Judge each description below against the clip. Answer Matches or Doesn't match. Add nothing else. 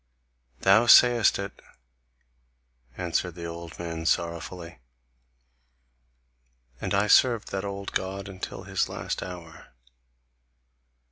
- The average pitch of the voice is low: Matches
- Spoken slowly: Matches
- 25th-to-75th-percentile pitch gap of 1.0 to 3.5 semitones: Matches